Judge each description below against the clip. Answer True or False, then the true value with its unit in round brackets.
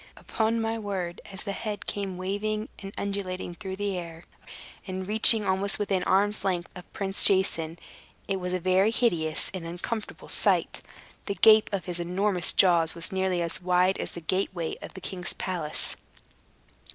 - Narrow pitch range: True (2.2 semitones)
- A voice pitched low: False (190 Hz)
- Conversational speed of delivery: True (165 wpm)